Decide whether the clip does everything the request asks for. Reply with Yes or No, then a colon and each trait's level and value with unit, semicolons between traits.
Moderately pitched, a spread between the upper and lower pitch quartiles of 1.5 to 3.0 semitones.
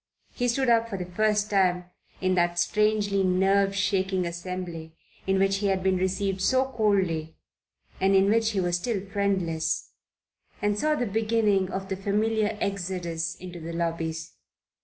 No: high, 195 Hz; average, 2.7 semitones